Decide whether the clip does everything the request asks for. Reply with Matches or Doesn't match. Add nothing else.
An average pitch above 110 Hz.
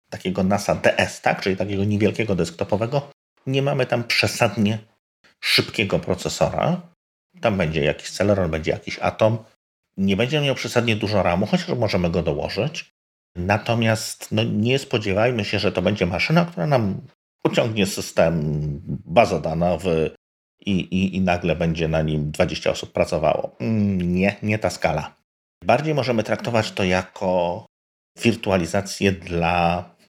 Doesn't match